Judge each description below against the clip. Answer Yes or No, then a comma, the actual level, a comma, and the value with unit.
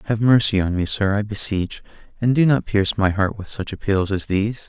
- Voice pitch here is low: Yes, low, 105 Hz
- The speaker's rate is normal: No, fast, 230 wpm